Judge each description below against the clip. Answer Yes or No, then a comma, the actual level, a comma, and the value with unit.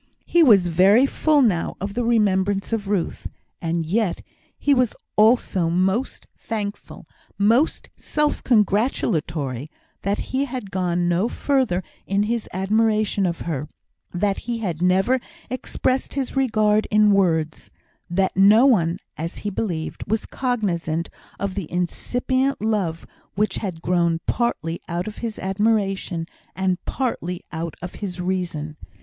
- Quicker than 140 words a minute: No, slow, 135 wpm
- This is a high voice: Yes, high, 200 Hz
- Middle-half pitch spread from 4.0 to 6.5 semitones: Yes, average, 4.5 semitones